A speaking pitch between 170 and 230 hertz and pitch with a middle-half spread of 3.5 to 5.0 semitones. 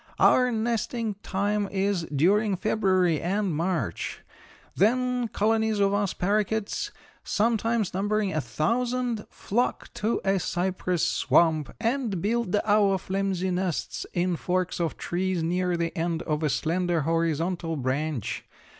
Yes: high, 190 Hz; average, 4.0 semitones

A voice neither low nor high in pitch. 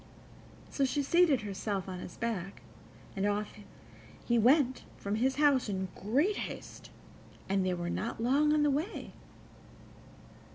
No: high, 235 Hz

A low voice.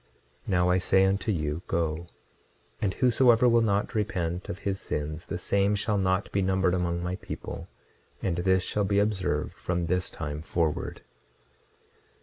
Yes: very low, 95 Hz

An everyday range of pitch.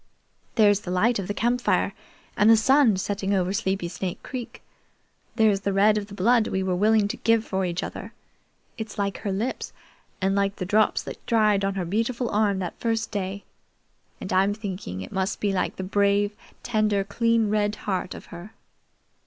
No: narrow, 2.3 semitones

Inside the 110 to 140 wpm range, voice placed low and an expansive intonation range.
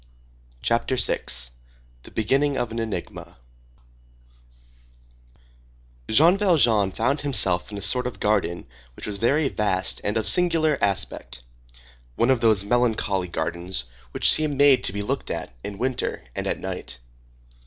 Yes: slow, 135 wpm; low, 110 Hz; wide, 6.0 semitones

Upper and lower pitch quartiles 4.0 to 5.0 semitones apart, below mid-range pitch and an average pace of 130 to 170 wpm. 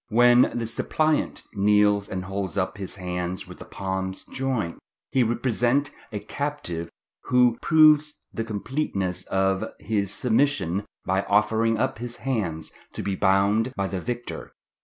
Yes: average, 4.3 semitones; low, 105 Hz; average, 140 wpm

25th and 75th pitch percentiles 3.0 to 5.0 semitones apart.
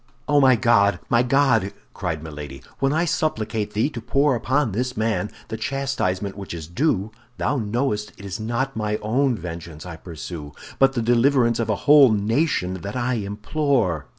No: wide, 5.6 semitones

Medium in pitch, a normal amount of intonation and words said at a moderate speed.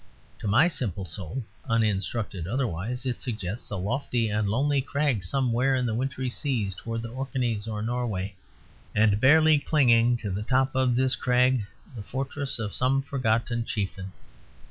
No: low, 120 Hz; average, 3.9 semitones; average, 155 wpm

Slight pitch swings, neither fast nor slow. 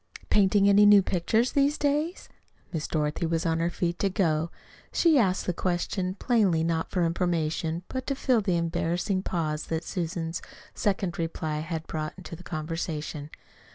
No: average, 3.4 semitones; average, 160 wpm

